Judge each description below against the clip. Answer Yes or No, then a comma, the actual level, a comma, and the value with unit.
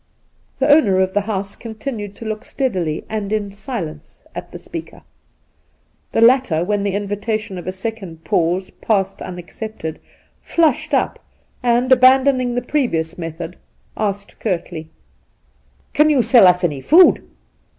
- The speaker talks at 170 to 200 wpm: No, average, 145 wpm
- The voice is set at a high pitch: Yes, high, 205 Hz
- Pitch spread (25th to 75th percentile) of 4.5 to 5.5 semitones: Yes, average, 5.2 semitones